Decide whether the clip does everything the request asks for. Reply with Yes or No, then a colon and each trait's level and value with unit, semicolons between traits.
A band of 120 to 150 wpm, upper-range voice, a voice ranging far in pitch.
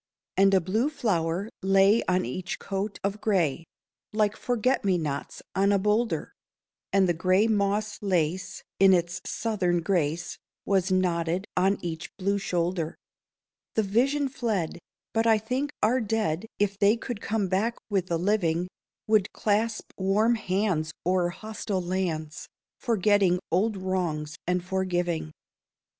No: average, 140 wpm; high, 195 Hz; average, 3.5 semitones